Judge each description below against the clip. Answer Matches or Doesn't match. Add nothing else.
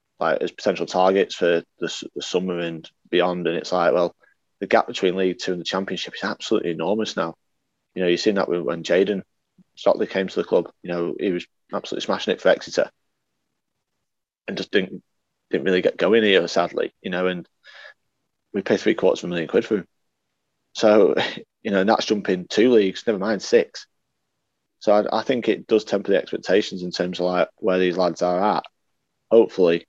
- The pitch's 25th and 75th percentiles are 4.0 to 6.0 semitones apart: Doesn't match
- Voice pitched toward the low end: Matches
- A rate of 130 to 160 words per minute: Doesn't match